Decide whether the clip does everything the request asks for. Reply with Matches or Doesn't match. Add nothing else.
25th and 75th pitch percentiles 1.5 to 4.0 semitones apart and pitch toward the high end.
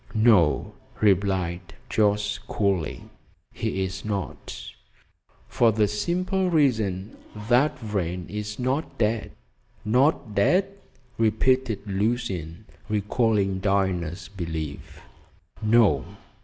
Doesn't match